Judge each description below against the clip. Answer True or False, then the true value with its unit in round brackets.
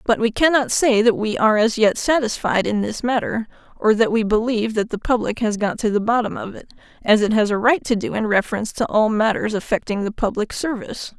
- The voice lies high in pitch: True (220 Hz)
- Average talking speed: False (225 wpm)